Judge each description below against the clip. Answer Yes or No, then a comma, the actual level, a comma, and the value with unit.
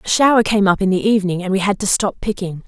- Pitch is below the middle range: No, high, 195 Hz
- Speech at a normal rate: No, fast, 290 wpm